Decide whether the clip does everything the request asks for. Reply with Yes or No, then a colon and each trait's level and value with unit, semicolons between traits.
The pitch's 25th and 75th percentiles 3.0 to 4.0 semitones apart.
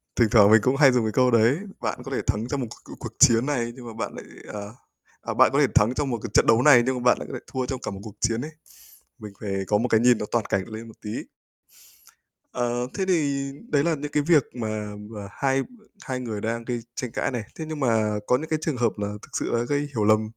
Yes: average, 3.5 semitones